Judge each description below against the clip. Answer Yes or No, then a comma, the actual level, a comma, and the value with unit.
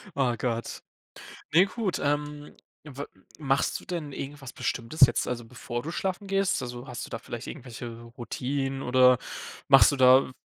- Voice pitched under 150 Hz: Yes, low, 135 Hz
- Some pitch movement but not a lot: Yes, average, 3.2 semitones